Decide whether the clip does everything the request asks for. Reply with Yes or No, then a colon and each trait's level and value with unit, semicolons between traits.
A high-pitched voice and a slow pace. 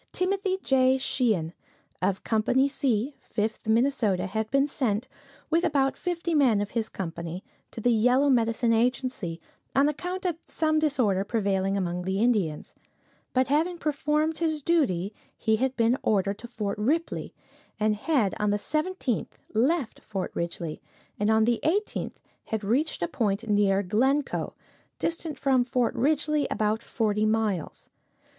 No: high, 235 Hz; average, 145 wpm